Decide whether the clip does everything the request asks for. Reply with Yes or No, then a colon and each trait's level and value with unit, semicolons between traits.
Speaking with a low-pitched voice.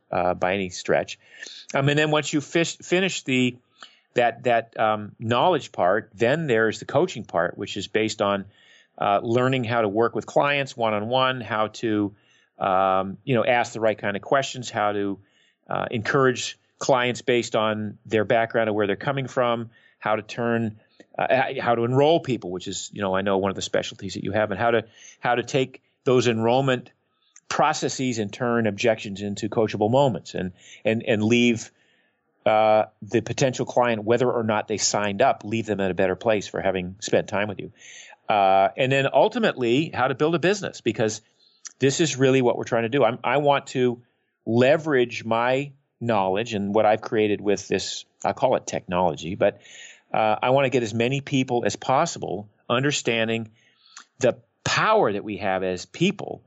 Yes: low, 115 Hz